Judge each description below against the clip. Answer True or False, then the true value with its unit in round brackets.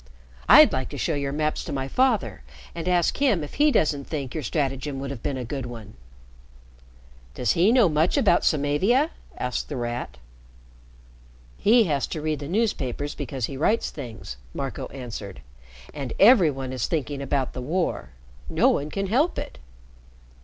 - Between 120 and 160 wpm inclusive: False (170 wpm)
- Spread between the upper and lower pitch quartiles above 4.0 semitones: True (5.2 semitones)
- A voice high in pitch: False (145 Hz)